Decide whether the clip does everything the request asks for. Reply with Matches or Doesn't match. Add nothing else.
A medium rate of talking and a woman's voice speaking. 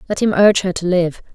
Doesn't match